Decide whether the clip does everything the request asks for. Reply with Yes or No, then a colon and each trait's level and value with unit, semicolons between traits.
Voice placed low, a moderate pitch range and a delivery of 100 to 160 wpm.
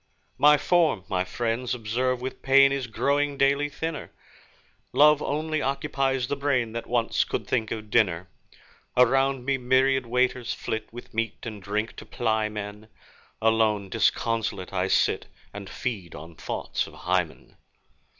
Yes: low, 120 Hz; average, 4.3 semitones; average, 145 wpm